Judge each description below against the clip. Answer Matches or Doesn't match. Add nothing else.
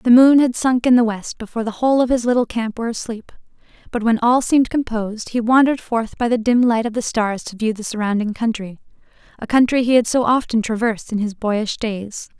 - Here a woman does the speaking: Matches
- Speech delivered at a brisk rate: Matches